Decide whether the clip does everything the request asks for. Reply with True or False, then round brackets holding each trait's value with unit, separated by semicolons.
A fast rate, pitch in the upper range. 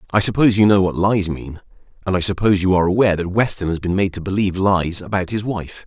False (245 wpm; 95 Hz)